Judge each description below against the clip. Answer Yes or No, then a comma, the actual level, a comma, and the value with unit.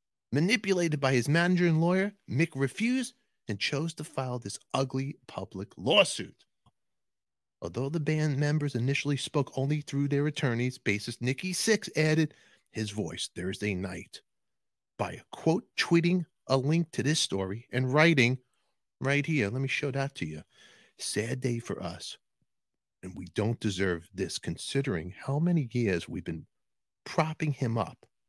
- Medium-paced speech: Yes, average, 150 wpm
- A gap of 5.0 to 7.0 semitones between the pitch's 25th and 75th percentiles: Yes, average, 5.3 semitones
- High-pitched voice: No, low, 135 Hz